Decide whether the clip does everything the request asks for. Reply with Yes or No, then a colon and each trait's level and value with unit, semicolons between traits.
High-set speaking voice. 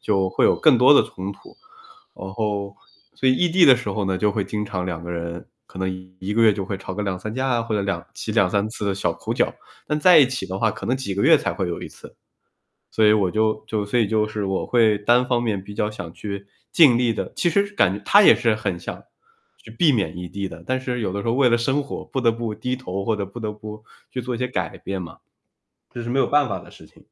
No: low, 105 Hz